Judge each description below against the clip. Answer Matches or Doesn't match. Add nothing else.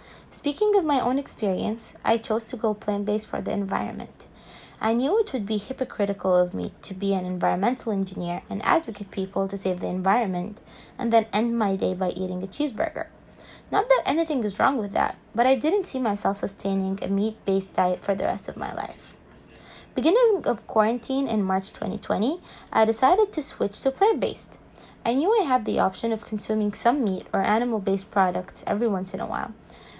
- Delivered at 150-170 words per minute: Doesn't match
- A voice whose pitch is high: Matches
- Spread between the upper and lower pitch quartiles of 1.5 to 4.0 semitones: Doesn't match